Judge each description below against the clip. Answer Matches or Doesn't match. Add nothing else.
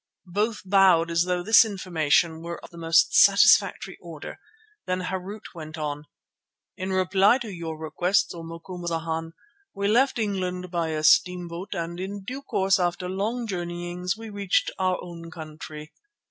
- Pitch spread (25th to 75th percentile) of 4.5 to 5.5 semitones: Doesn't match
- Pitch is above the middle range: Doesn't match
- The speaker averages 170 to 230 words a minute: Doesn't match